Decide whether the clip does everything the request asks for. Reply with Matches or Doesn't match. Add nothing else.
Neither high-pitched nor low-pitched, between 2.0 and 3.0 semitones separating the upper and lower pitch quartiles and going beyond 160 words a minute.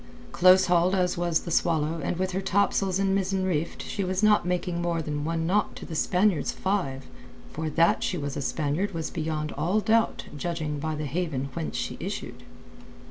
Doesn't match